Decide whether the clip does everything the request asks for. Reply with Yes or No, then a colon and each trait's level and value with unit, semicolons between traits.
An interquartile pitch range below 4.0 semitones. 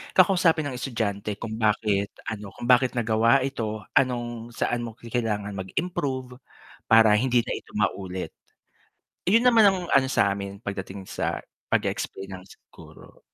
No: average, 4.3 semitones